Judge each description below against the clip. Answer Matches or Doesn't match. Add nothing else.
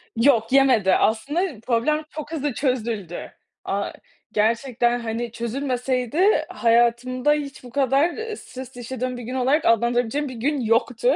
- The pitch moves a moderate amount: Matches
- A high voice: Matches